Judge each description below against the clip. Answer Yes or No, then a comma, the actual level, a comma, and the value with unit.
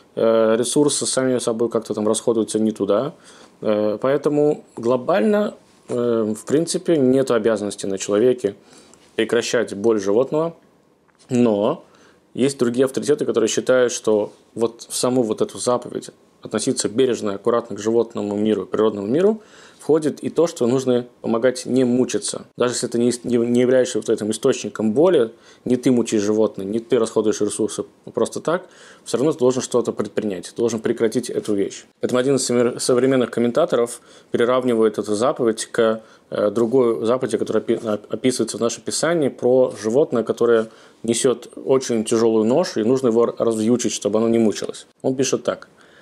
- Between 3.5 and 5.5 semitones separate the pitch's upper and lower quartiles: No, narrow, 2.4 semitones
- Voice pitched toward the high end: No, low, 115 Hz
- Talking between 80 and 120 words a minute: No, average, 145 wpm